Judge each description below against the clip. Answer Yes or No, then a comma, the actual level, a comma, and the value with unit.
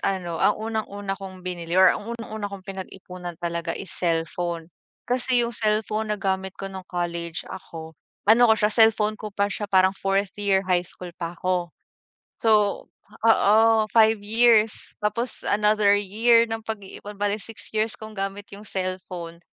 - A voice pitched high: Yes, high, 200 Hz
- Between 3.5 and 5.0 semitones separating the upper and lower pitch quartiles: No, average, 2.9 semitones